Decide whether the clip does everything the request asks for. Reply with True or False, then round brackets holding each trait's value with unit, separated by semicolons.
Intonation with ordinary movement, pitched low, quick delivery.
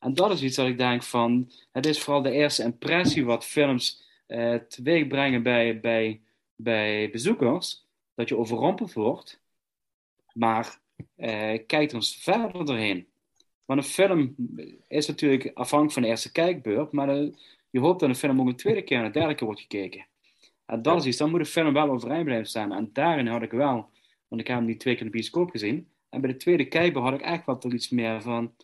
True (4.1 semitones; 130 Hz; 210 wpm)